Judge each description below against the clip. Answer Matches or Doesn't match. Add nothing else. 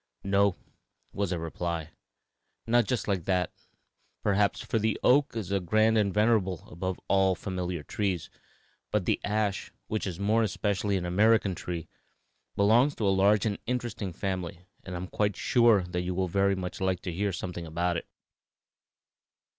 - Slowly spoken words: Doesn't match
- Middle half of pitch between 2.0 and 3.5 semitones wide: Matches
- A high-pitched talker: Doesn't match